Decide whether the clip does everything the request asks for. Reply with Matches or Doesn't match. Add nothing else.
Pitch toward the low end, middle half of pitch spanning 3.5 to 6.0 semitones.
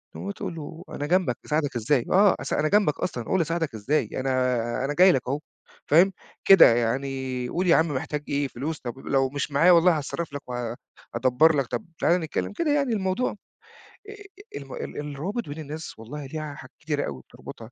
Doesn't match